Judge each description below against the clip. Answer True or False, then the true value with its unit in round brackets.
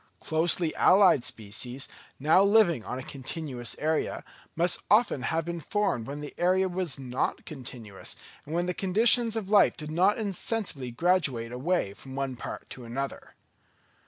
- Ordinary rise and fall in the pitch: False (6.3 semitones)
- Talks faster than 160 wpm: False (155 wpm)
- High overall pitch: False (160 Hz)